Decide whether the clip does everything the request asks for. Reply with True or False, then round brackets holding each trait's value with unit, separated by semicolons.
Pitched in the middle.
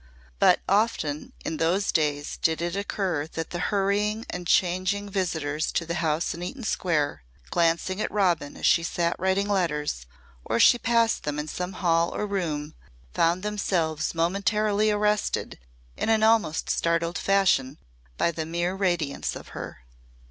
True (175 Hz)